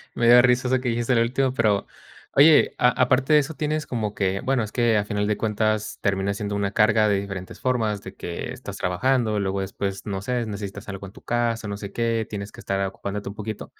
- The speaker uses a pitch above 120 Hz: No, low, 110 Hz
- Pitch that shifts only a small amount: No, average, 3.5 semitones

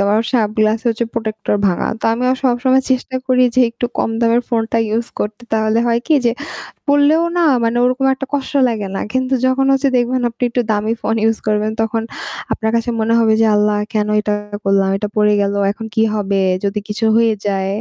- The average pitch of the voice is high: Yes, high, 225 Hz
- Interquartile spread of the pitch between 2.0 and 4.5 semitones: Yes, average, 2.9 semitones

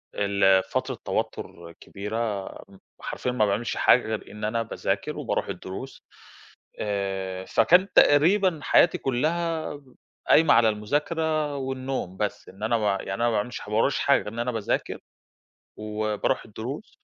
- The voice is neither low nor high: No, low, 115 Hz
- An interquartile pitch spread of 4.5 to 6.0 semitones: Yes, wide, 5.4 semitones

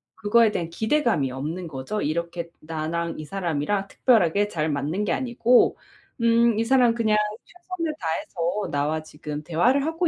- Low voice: No, medium, 185 Hz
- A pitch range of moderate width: No, wide, 6.7 semitones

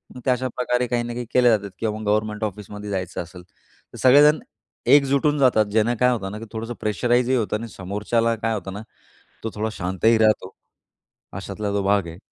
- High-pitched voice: No, low, 110 Hz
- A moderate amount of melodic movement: Yes, average, 3.2 semitones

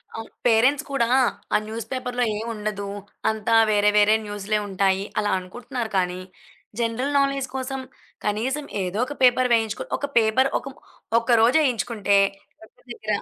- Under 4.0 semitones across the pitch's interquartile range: Yes, average, 3.6 semitones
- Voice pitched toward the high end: Yes, high, 225 Hz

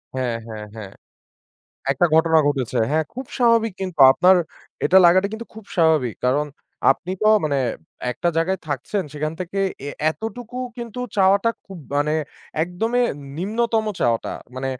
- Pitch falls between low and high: Yes, medium, 175 Hz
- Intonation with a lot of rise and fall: Yes, wide, 7.0 semitones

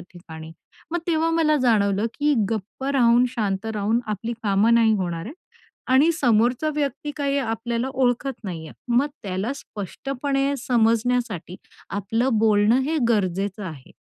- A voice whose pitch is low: No, high, 230 Hz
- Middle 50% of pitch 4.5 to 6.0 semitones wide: Yes, average, 5.0 semitones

